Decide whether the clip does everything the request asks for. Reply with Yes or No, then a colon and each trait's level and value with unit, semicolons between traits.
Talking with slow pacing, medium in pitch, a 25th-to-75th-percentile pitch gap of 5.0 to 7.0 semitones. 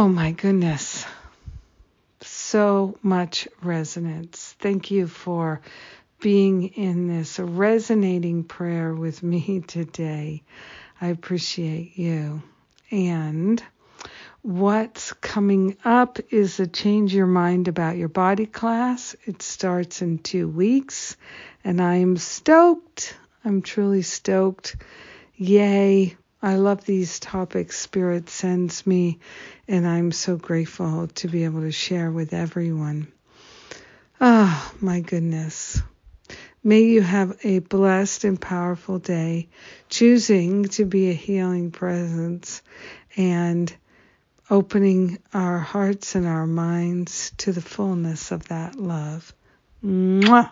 No: slow, 115 wpm; medium, 180 Hz; average, 2.9 semitones